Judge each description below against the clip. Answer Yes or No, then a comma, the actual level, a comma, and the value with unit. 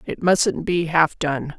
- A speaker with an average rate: Yes, average, 190 wpm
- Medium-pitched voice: Yes, medium, 165 Hz